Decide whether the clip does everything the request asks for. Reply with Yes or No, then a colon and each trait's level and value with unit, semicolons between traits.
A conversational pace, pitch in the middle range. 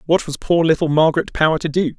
No: fast, 240 wpm; medium, 160 Hz